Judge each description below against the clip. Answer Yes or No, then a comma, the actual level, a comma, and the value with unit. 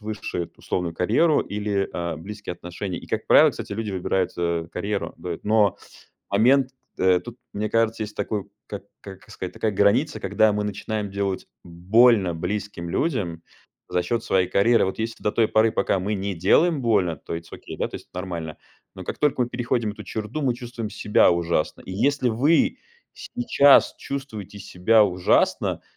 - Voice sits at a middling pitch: No, low, 105 Hz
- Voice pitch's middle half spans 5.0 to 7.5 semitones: No, average, 4.0 semitones